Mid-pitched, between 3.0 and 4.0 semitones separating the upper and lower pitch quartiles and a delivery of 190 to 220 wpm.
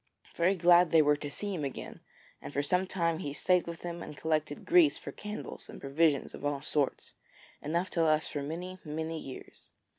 Yes: medium, 160 Hz; average, 3.3 semitones; average, 200 wpm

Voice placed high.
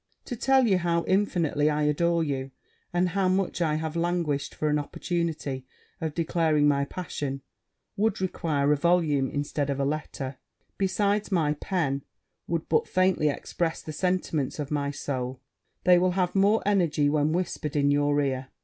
No: medium, 155 Hz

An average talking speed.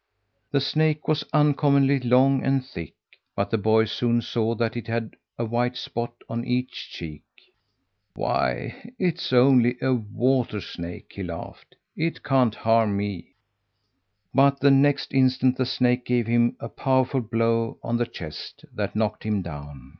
Yes: average, 155 wpm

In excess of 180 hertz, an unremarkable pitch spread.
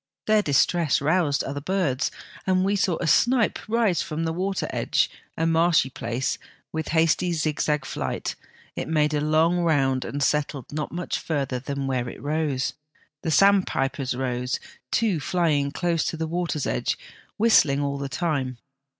No: medium, 155 Hz; average, 3.9 semitones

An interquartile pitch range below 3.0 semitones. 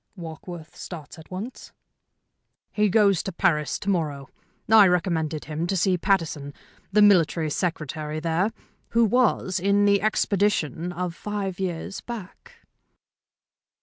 No: average, 3.9 semitones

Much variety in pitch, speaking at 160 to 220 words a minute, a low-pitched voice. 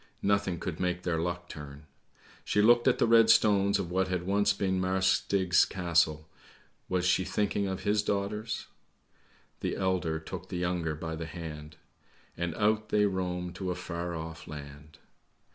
No: average, 3.1 semitones; average, 170 wpm; very low, 90 Hz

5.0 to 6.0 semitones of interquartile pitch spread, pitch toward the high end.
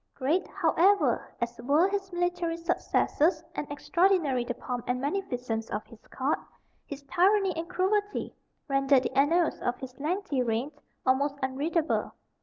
Yes: wide, 5.6 semitones; very high, 295 Hz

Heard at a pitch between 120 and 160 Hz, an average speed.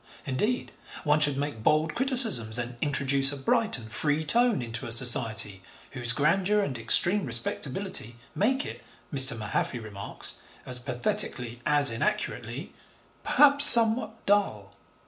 No: medium, 140 Hz; slow, 130 wpm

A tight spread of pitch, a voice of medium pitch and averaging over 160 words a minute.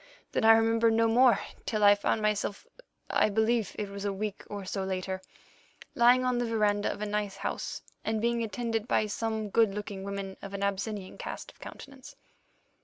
No: narrow, 2.2 semitones; high, 210 Hz; average, 180 wpm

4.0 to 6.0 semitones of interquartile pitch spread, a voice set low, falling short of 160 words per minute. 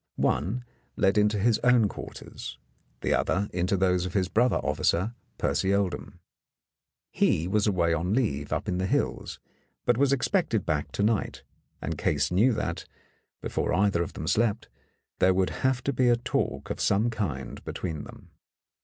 No: average, 4.4 semitones; low, 100 Hz; average, 165 wpm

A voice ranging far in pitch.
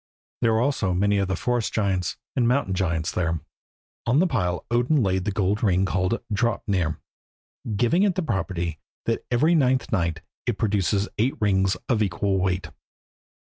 No: average, 4.6 semitones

